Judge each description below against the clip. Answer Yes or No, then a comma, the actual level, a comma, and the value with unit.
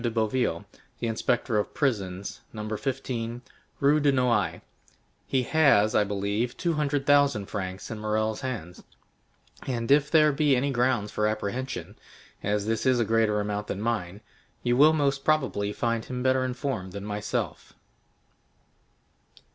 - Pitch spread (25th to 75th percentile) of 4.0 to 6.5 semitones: Yes, average, 4.4 semitones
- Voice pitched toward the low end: Yes, low, 115 Hz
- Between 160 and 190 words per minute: No, average, 145 wpm